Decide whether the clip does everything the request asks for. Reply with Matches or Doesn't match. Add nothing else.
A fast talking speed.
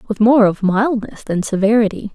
Doesn't match